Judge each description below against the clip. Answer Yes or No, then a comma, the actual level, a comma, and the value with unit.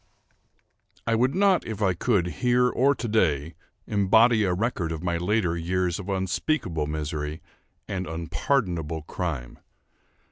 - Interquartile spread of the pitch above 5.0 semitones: Yes, wide, 5.6 semitones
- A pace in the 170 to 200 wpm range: No, slow, 135 wpm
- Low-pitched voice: Yes, very low, 95 Hz